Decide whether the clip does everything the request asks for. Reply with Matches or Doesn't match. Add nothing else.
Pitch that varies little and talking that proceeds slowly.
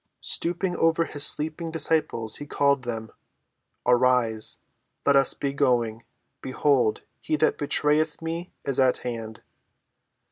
Doesn't match